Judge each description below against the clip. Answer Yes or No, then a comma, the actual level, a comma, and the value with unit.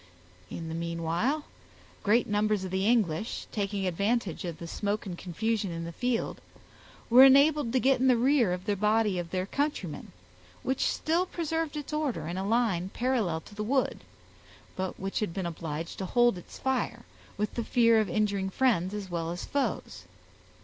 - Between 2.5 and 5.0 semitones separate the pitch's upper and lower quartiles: No, wide, 5.5 semitones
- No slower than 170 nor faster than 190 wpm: Yes, average, 180 wpm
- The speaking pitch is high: Yes, high, 210 Hz